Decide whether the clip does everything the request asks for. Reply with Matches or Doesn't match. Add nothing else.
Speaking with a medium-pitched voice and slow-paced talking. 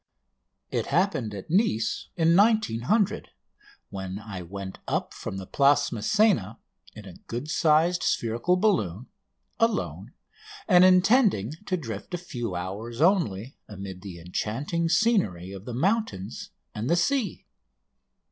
Doesn't match